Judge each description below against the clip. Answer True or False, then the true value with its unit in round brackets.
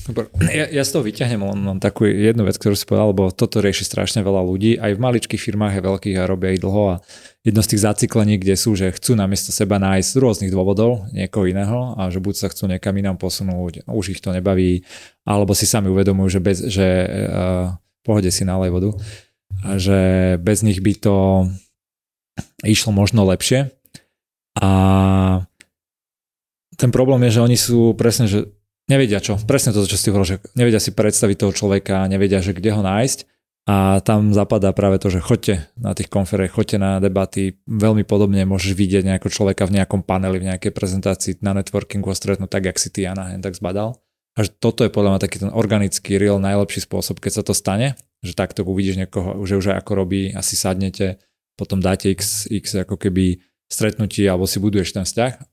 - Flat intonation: True (1.9 semitones)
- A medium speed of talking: False (200 wpm)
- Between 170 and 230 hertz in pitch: False (100 Hz)